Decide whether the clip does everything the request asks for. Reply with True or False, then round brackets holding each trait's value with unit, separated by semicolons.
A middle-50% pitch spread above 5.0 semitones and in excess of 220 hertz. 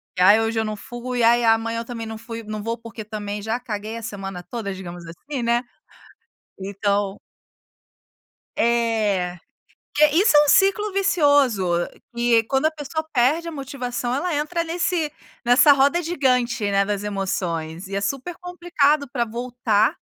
True (5.4 semitones; 235 Hz)